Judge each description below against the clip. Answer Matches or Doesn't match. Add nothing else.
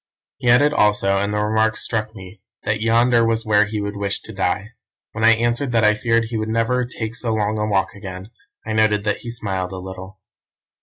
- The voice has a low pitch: Matches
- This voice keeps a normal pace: Doesn't match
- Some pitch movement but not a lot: Doesn't match